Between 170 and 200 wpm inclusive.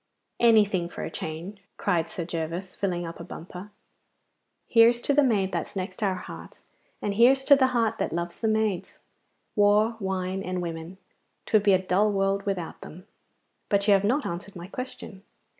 Yes: average, 175 wpm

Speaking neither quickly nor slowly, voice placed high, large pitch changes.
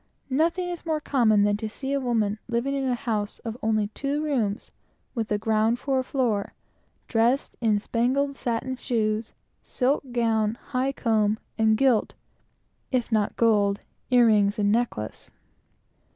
No: average, 150 wpm; high, 230 Hz; average, 3.5 semitones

